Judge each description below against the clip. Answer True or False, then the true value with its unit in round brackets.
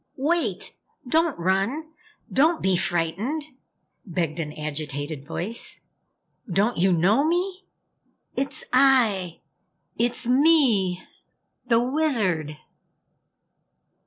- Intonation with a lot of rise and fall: True (8.4 semitones)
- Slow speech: True (85 wpm)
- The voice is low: False (210 Hz)